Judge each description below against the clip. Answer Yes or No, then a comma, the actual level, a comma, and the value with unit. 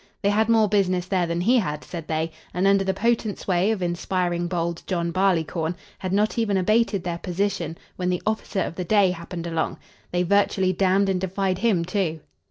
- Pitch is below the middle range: No, medium, 185 Hz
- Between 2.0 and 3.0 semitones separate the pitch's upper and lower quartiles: Yes, narrow, 2.5 semitones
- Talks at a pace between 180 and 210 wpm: Yes, average, 195 wpm